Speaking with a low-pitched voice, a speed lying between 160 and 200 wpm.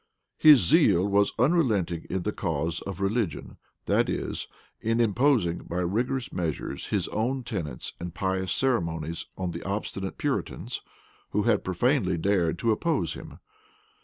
No: low, 100 Hz; average, 140 wpm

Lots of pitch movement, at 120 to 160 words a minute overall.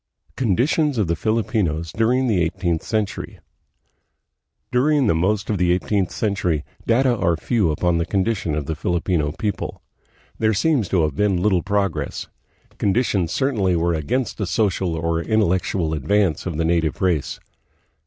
No: average, 4.7 semitones; average, 155 wpm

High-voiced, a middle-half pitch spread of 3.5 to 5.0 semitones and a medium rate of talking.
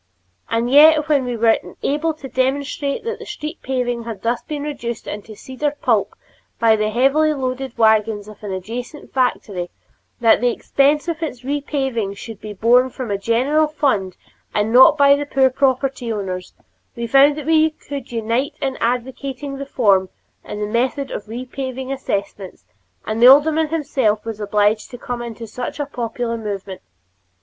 Yes: very high, 250 Hz; average, 4.1 semitones; average, 170 wpm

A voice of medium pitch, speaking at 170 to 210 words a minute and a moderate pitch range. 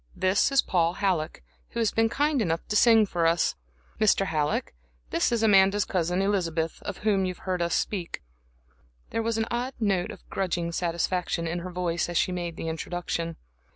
Yes: medium, 180 Hz; average, 185 wpm; average, 3.6 semitones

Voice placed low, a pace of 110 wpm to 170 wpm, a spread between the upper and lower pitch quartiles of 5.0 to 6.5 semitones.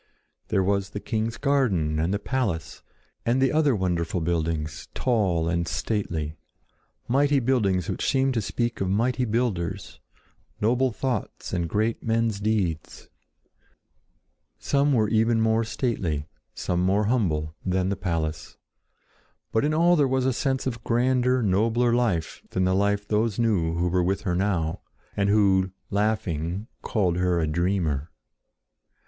Yes: low, 100 Hz; average, 140 wpm; average, 5.3 semitones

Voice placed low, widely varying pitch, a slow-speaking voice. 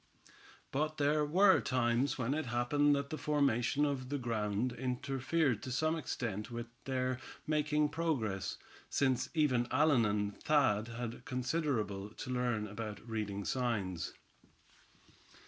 No: low, 125 Hz; average, 4.3 semitones; slow, 130 wpm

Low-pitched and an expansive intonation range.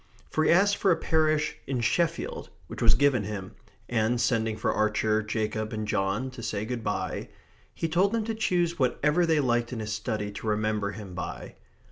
Yes: low, 115 Hz; wide, 6.5 semitones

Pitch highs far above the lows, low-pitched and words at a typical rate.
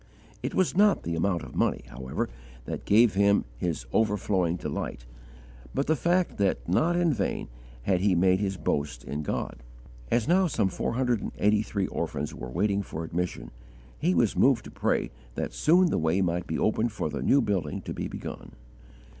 Yes: wide, 6.0 semitones; low, 100 Hz; average, 190 wpm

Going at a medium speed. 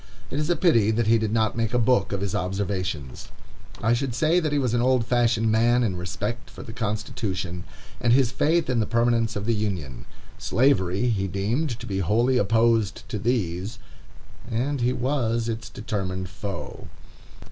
Yes: average, 180 wpm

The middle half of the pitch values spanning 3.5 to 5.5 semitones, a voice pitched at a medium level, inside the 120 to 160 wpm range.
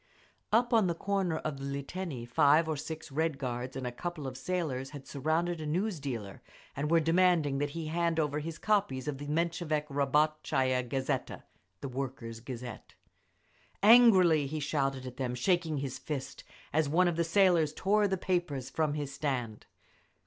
No: average, 4.0 semitones; medium, 150 Hz; average, 170 wpm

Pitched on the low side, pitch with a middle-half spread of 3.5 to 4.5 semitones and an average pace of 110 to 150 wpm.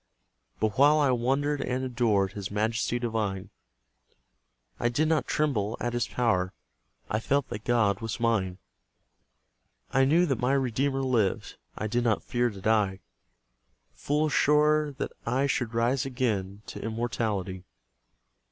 Yes: low, 120 Hz; average, 4.1 semitones; average, 140 wpm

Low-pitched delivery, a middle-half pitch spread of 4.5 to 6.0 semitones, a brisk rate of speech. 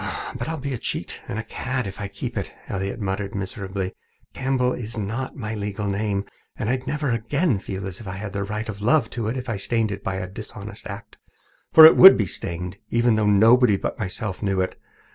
No: low, 105 Hz; average, 3.8 semitones; fast, 220 wpm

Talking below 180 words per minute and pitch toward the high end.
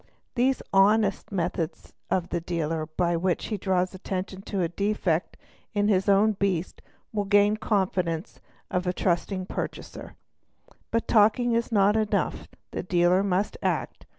Yes: average, 150 wpm; high, 195 Hz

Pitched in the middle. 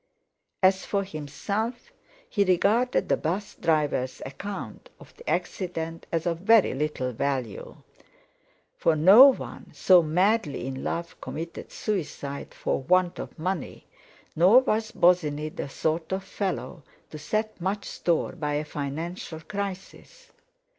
Yes: medium, 175 Hz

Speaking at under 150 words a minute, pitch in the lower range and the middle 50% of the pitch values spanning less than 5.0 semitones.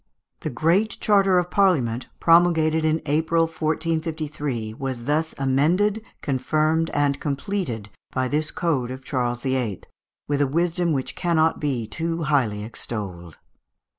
No: slow, 135 wpm; medium, 150 Hz; average, 4.2 semitones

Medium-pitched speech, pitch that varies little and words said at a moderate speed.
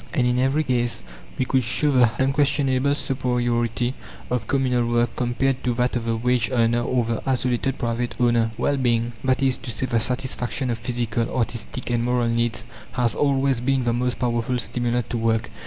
No: low, 125 Hz; narrow, 1.7 semitones; average, 185 wpm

